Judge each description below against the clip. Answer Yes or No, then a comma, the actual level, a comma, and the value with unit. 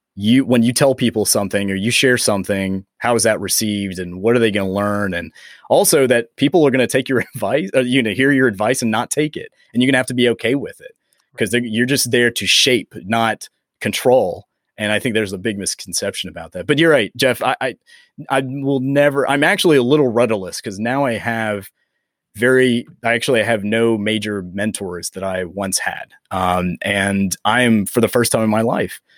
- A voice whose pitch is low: Yes, low, 115 Hz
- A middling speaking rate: No, fast, 220 wpm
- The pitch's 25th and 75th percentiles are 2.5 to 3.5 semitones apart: No, average, 4.1 semitones